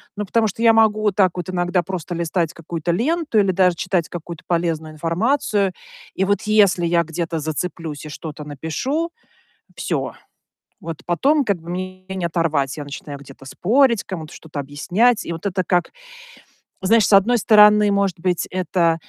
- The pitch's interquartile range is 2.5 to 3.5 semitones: No, average, 3.9 semitones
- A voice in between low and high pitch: Yes, medium, 180 Hz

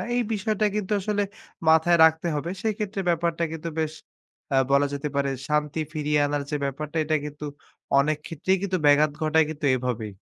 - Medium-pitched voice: Yes, medium, 155 Hz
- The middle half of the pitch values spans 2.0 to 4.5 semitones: Yes, average, 3.0 semitones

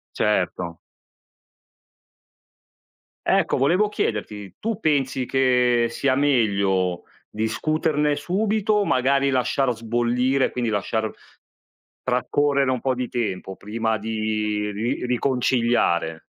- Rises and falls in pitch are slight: No, average, 4.2 semitones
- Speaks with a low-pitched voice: Yes, low, 125 Hz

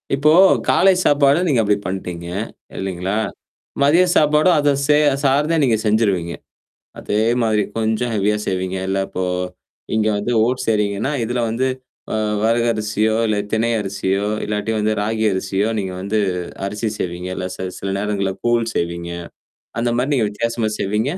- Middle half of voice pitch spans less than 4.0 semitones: Yes, average, 3.5 semitones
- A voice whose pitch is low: Yes, low, 110 Hz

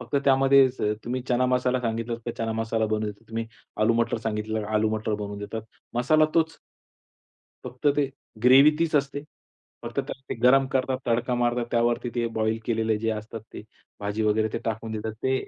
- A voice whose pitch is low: Yes, low, 115 Hz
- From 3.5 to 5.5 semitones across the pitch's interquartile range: No, average, 2.7 semitones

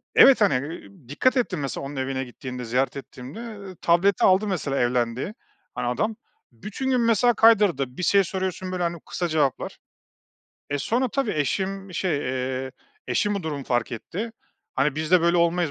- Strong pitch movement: Yes, wide, 6.9 semitones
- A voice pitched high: No, medium, 170 Hz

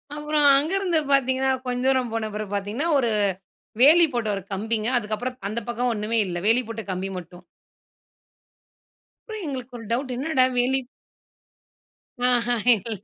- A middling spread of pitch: Yes, average, 3.6 semitones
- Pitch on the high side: Yes, high, 245 Hz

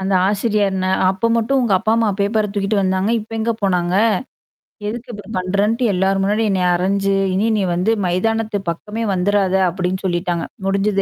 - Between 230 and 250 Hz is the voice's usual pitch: No, high, 200 Hz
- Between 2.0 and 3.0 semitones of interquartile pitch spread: Yes, narrow, 2.5 semitones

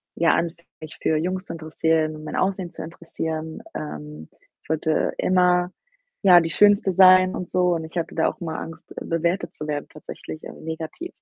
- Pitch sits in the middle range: Yes, medium, 165 Hz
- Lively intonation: No, narrow, 2.5 semitones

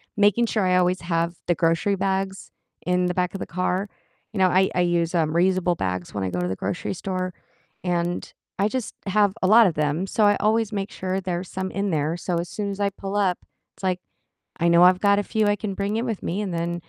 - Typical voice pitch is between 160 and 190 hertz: Yes, medium, 185 Hz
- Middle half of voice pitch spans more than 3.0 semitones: No, narrow, 2.6 semitones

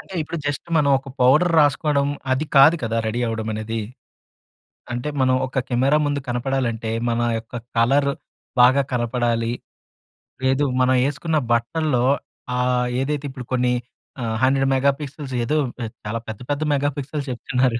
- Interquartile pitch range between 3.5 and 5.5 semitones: No, average, 3.1 semitones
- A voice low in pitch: Yes, low, 130 Hz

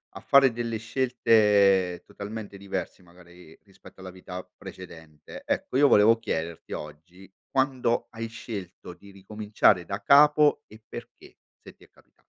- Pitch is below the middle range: Yes, low, 100 Hz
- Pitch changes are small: No, average, 4.1 semitones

